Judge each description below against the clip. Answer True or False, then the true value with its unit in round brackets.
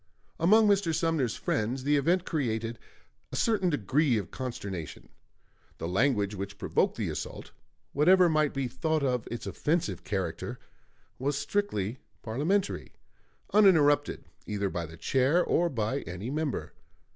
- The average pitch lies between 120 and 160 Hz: True (135 Hz)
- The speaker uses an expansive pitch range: True (7.4 semitones)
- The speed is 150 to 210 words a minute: False (135 wpm)